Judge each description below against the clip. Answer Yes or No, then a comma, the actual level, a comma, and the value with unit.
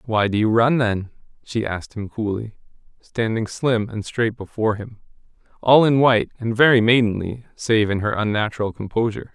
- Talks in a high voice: No, low, 110 Hz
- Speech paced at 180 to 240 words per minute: No, average, 165 wpm